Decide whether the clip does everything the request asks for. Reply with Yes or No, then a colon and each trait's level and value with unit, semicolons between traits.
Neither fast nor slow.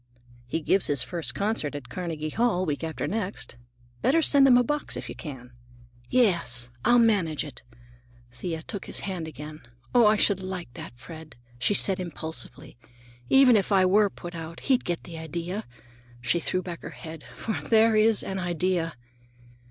Yes: average, 170 wpm